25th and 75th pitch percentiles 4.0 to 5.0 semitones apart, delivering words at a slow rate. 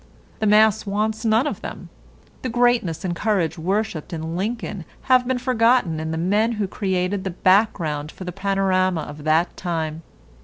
No: average, 4.7 semitones; average, 165 wpm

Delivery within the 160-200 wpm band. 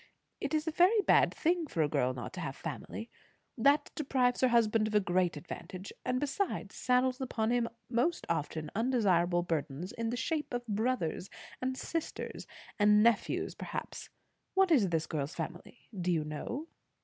Yes: average, 170 wpm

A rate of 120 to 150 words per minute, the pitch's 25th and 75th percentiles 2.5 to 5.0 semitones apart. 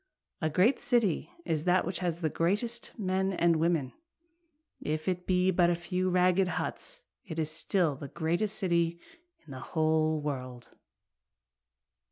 Yes: average, 145 wpm; average, 2.9 semitones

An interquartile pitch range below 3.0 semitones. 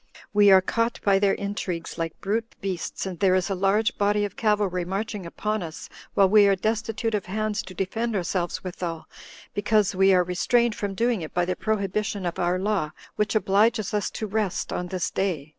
Yes: narrow, 2.6 semitones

